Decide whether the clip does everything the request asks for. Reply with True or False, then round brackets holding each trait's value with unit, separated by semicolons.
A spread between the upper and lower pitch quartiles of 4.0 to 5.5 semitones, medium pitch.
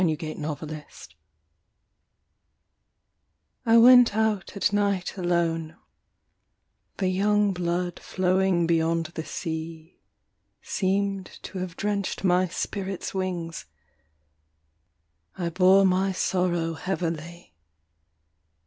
False (2.7 semitones; 180 Hz)